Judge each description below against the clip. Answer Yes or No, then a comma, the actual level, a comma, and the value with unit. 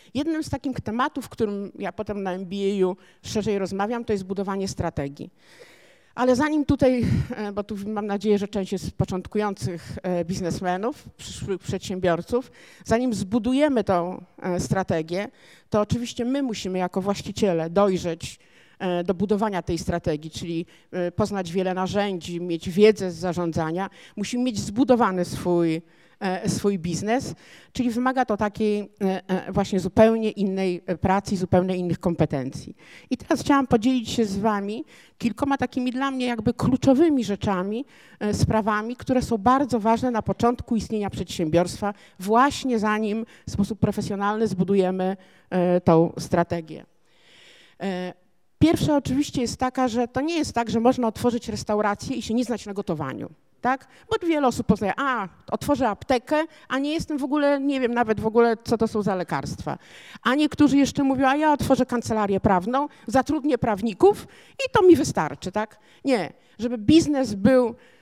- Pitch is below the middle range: No, high, 210 Hz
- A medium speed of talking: Yes, average, 145 wpm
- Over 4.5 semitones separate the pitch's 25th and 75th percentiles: Yes, average, 5.2 semitones